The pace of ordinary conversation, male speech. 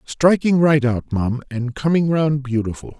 Yes: average, 160 wpm; male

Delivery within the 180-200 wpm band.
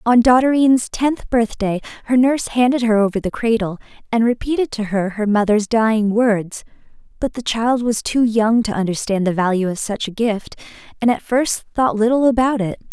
Yes: average, 185 wpm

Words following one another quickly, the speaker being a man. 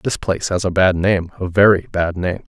Yes: fast, 210 wpm; male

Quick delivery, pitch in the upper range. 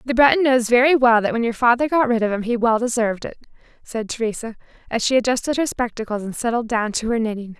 Yes: fast, 235 wpm; high, 235 Hz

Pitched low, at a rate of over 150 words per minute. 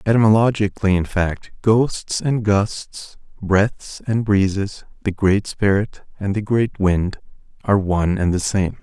No: low, 100 Hz; average, 145 wpm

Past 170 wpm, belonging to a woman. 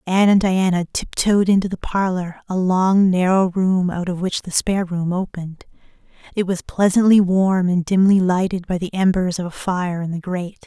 Yes: average, 190 wpm; female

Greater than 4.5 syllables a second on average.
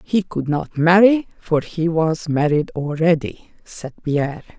No: 4.0 syllables/s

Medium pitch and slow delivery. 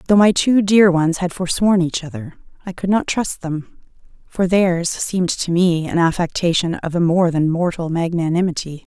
No: medium, 175 Hz; average, 180 wpm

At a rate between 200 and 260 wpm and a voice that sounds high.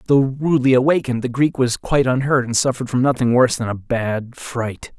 No: fast, 205 wpm; low, 125 Hz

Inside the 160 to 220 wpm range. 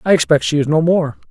No: fast, 275 wpm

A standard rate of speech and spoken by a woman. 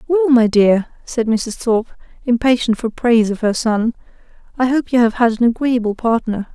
Yes: average, 185 wpm; female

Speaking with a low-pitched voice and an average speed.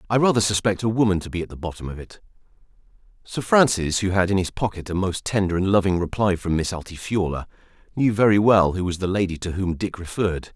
No: very low, 95 Hz; fast, 220 wpm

